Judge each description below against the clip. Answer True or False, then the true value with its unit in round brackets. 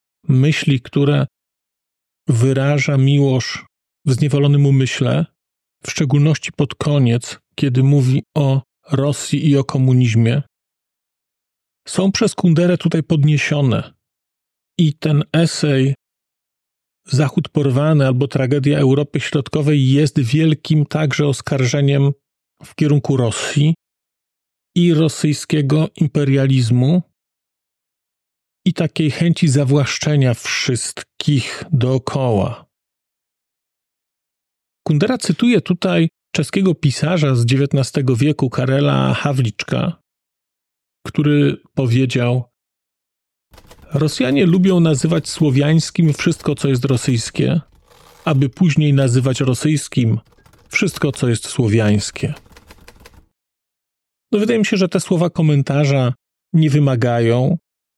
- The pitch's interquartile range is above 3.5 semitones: False (3.0 semitones)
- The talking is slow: True (90 wpm)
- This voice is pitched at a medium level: True (145 Hz)